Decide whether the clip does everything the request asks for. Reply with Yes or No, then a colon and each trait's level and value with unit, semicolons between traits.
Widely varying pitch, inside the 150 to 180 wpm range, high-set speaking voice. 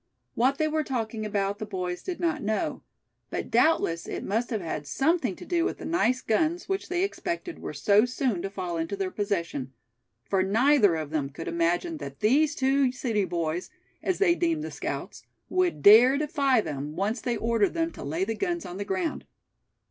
No: wide, 8.9 semitones; average, 195 wpm; high, 225 Hz